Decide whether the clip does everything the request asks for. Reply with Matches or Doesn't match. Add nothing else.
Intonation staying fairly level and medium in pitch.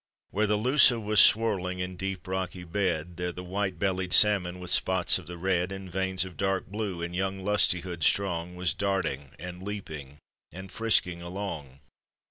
Doesn't match